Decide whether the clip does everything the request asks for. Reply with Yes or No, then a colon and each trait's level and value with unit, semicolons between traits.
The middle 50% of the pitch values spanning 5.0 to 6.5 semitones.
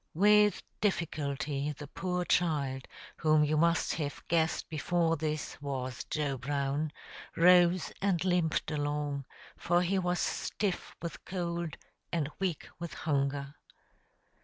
No: average, 3.4 semitones